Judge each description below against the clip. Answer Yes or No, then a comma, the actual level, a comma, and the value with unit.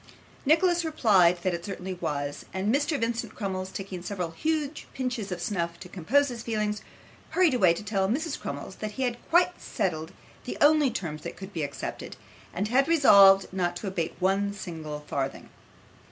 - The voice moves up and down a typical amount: No, wide, 6.4 semitones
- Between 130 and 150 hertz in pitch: No, high, 195 Hz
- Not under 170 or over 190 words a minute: Yes, average, 175 wpm